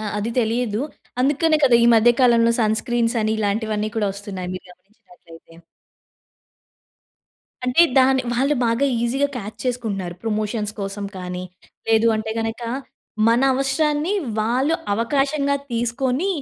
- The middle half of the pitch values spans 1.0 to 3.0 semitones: No, average, 3.7 semitones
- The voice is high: Yes, high, 230 Hz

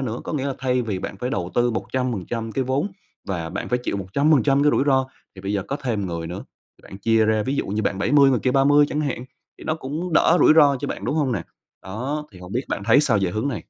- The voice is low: Yes, low, 125 Hz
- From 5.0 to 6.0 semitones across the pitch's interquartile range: Yes, wide, 5.6 semitones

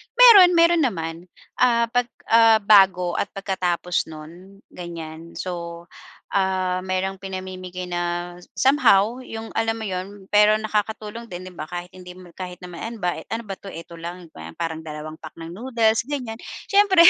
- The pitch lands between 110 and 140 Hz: No, high, 190 Hz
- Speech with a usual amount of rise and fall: Yes, average, 4.3 semitones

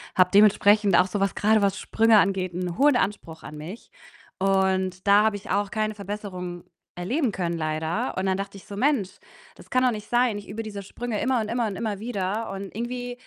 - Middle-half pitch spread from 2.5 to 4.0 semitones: Yes, average, 2.8 semitones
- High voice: Yes, high, 200 Hz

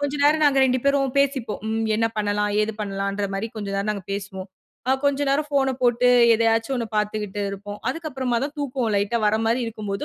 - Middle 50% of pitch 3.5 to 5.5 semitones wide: Yes, average, 4.6 semitones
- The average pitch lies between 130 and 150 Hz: No, high, 225 Hz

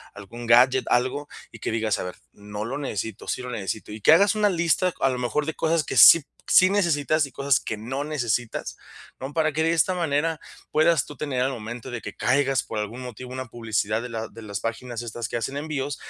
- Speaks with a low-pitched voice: Yes, low, 130 Hz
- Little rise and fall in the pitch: No, average, 4.8 semitones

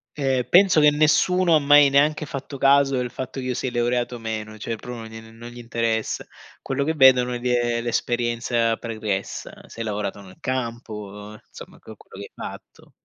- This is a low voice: Yes, low, 120 Hz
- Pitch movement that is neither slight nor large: Yes, average, 3.2 semitones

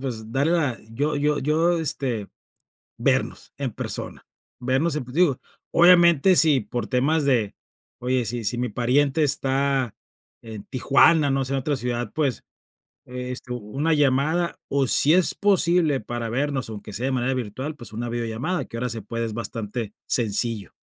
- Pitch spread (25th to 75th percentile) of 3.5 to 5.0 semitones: Yes, average, 3.9 semitones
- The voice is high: No, low, 130 Hz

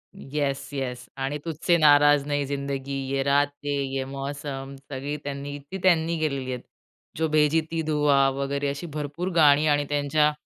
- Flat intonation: Yes, narrow, 1.5 semitones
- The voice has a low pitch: No, medium, 145 Hz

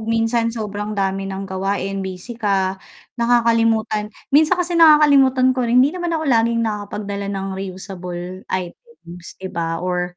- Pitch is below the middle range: No, high, 210 Hz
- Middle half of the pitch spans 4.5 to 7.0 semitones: No, average, 4.1 semitones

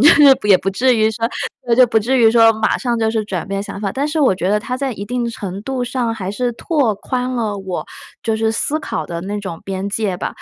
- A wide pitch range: No, average, 3.8 semitones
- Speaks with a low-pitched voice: No, high, 225 Hz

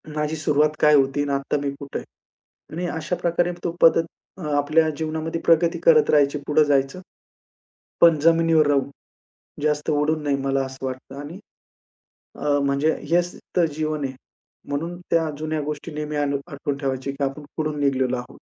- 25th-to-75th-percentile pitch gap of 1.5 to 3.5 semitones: Yes, narrow, 2.4 semitones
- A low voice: No, medium, 150 Hz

